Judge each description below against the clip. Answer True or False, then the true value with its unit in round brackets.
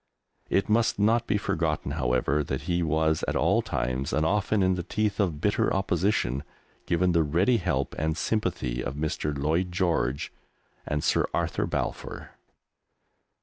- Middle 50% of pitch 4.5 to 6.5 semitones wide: True (5.0 semitones)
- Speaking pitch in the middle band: False (80 Hz)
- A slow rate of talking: False (150 wpm)